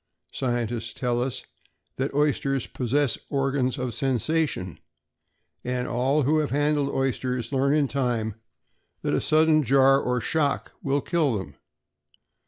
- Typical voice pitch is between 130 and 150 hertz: Yes, low, 135 Hz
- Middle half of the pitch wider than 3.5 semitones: No, average, 2.7 semitones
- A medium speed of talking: No, slow, 130 wpm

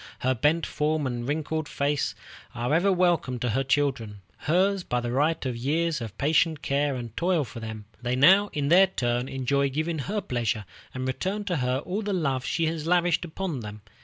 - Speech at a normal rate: Yes, average, 195 wpm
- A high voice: No, medium, 145 Hz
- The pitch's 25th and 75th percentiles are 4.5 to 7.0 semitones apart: Yes, average, 5.1 semitones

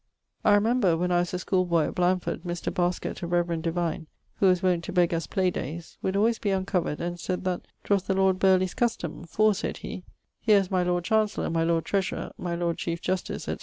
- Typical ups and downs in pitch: No, narrow, 1.9 semitones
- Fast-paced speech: Yes, fast, 220 wpm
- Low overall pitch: No, medium, 180 Hz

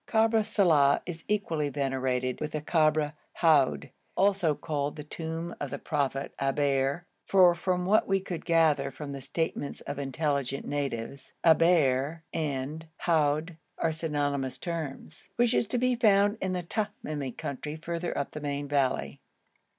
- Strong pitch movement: No, average, 3.7 semitones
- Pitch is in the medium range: Yes, medium, 155 Hz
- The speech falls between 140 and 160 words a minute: Yes, average, 150 wpm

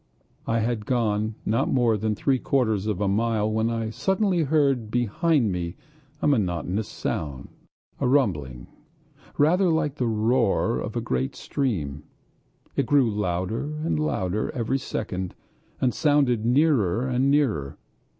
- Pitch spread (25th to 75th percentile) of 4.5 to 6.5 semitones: Yes, average, 5.1 semitones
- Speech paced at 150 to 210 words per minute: No, average, 140 wpm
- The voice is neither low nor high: No, low, 115 Hz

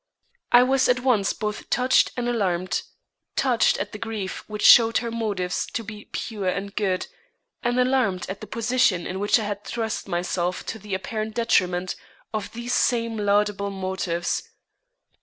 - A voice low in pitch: No, high, 210 Hz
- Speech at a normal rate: Yes, average, 160 wpm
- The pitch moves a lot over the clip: No, average, 3.5 semitones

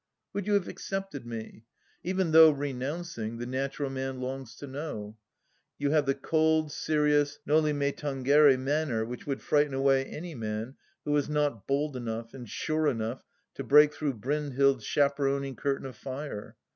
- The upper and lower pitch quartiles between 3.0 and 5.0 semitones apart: No, narrow, 2.6 semitones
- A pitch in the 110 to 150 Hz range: Yes, medium, 140 Hz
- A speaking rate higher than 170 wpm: No, average, 160 wpm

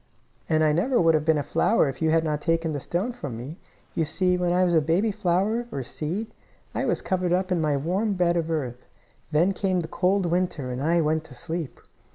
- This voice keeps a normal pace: No, fast, 230 wpm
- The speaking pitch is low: No, medium, 170 Hz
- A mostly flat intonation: No, average, 3.1 semitones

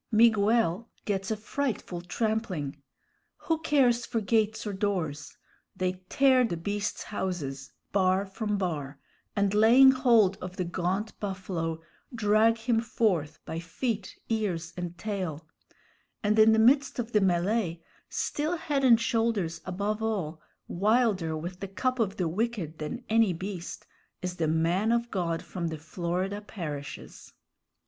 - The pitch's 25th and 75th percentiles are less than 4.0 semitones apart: No, average, 4.6 semitones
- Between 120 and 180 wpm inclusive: Yes, average, 140 wpm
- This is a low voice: No, high, 200 Hz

